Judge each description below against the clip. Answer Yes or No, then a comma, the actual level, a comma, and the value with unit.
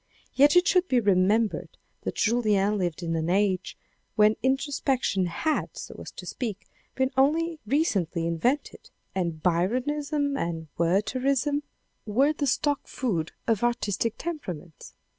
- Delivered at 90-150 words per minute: Yes, slow, 135 wpm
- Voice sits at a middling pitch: No, high, 230 Hz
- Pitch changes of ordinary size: No, wide, 7.4 semitones